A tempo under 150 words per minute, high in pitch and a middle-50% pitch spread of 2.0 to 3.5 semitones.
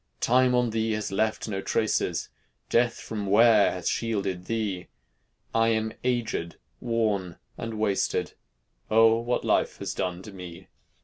No: average, 140 wpm; low, 110 Hz; average, 2.9 semitones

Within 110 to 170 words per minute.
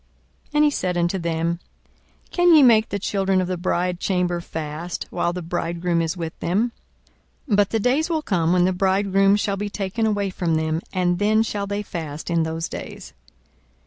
No: average, 190 wpm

